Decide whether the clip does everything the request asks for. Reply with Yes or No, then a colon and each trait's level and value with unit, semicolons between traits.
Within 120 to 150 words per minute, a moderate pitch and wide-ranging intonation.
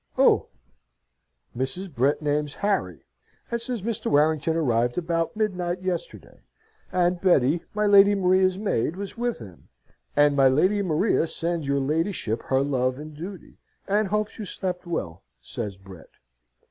Yes: average, 145 wpm; medium, 170 Hz; wide, 5.8 semitones